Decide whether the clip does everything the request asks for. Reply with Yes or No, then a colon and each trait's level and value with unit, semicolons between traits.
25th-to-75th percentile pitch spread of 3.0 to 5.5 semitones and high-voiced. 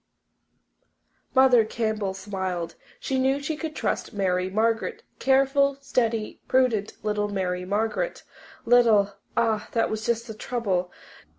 Yes: average, 4.1 semitones; high, 220 Hz